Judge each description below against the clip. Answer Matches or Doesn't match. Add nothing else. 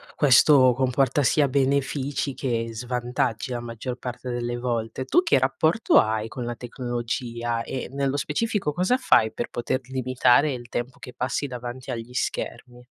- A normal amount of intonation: Doesn't match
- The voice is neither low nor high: Doesn't match